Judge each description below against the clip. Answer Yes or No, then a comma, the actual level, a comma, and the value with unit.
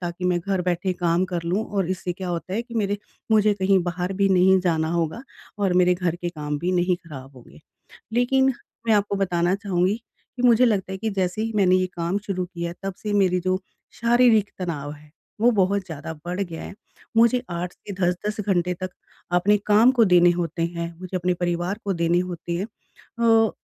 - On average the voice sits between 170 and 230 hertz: Yes, medium, 185 Hz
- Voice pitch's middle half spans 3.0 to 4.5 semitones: No, narrow, 2.6 semitones